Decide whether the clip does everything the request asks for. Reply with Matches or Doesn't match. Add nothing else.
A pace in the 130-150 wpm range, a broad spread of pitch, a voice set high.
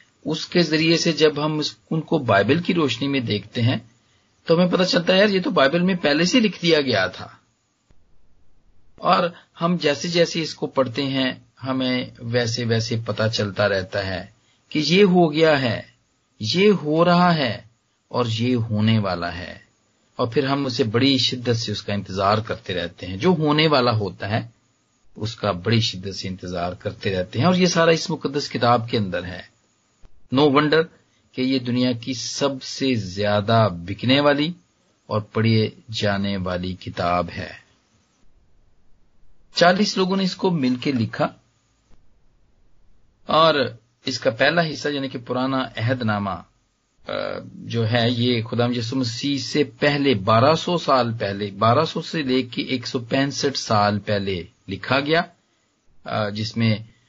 Doesn't match